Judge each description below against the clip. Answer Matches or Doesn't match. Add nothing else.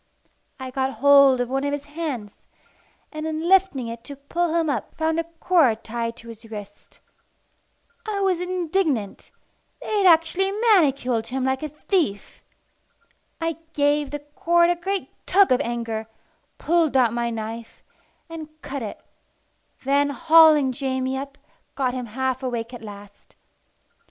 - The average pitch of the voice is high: Matches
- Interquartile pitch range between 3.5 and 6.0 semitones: Matches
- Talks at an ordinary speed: Matches